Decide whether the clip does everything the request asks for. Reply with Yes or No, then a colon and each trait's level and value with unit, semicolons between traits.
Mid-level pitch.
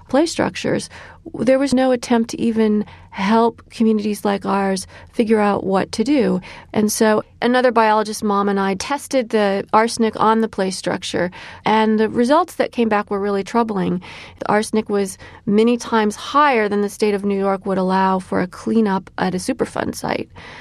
No: high, 215 Hz